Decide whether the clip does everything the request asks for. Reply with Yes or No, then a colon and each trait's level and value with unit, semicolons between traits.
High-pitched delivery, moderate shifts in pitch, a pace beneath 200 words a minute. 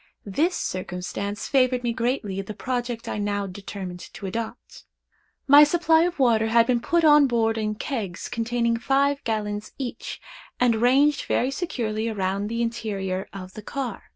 Yes: high, 230 Hz; average, 4.0 semitones; average, 160 wpm